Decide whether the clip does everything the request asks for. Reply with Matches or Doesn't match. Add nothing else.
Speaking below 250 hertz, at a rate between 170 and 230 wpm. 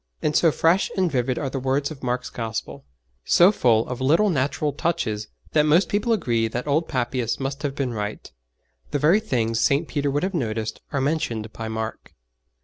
Matches